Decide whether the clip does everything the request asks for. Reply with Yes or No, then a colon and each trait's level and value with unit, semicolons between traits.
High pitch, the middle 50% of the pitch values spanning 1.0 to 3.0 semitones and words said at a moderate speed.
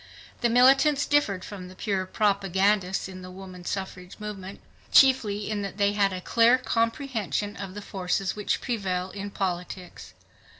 Yes: high, 200 Hz; average, 2.7 semitones; average, 155 wpm